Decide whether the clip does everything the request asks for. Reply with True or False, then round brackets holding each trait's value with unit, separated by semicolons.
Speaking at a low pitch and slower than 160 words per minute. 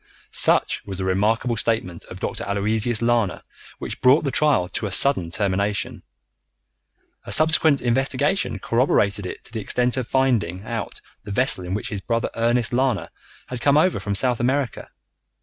False (115 Hz; 165 wpm)